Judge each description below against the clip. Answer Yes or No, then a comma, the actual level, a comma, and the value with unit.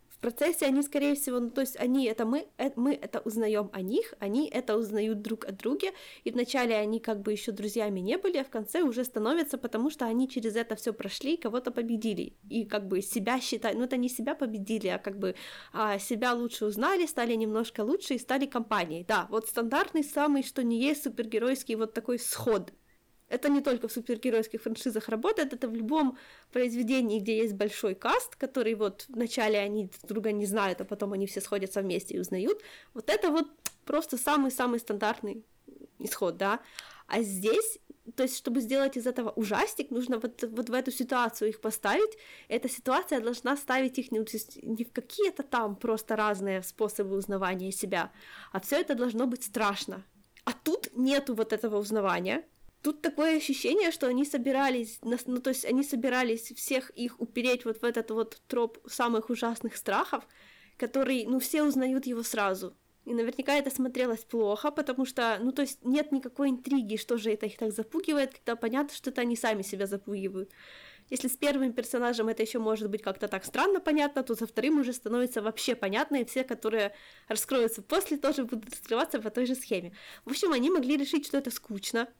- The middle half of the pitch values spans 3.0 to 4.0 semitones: Yes, average, 3.6 semitones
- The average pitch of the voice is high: Yes, high, 240 Hz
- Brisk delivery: Yes, fast, 185 wpm